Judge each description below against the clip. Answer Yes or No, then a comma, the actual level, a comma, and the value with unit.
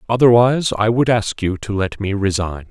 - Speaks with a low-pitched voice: Yes, low, 110 Hz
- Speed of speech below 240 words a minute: Yes, average, 200 wpm